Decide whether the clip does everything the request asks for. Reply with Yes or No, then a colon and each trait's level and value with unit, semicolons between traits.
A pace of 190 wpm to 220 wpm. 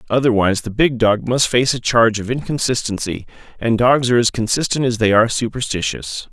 No: average, 180 wpm